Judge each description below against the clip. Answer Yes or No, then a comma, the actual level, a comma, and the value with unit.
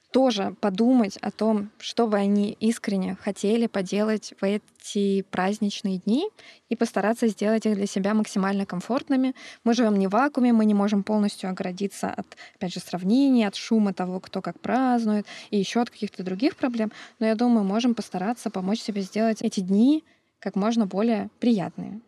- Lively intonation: No, average, 2.7 semitones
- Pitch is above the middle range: Yes, high, 215 Hz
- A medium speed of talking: No, fast, 170 wpm